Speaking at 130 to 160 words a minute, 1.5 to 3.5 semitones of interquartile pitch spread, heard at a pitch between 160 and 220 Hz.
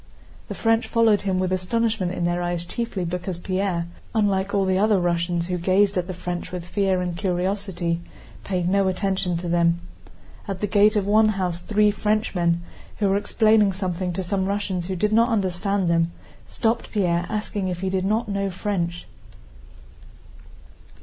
No: average, 170 wpm; average, 2.7 semitones; high, 190 Hz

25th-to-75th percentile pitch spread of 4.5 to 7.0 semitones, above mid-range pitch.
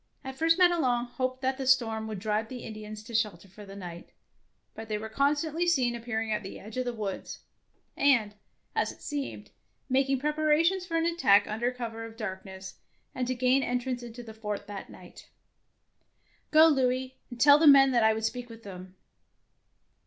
No: average, 4.0 semitones; high, 245 Hz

